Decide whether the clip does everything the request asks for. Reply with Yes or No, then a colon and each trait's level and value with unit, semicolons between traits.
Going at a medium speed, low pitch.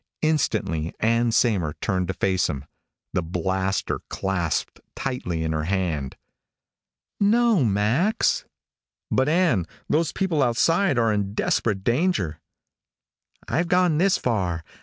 No: slow, 120 wpm; low, 110 Hz